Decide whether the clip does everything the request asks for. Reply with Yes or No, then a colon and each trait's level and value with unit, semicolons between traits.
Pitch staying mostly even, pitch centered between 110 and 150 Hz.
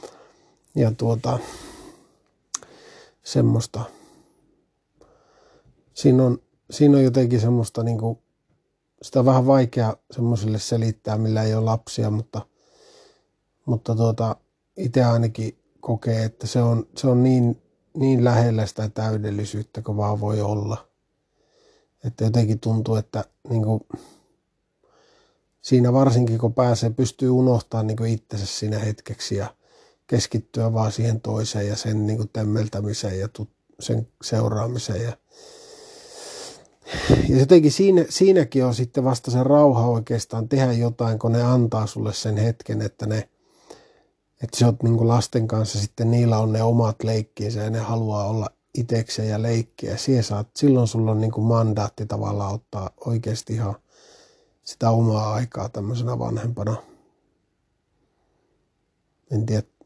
Yes: narrow, 2.1 semitones; low, 115 Hz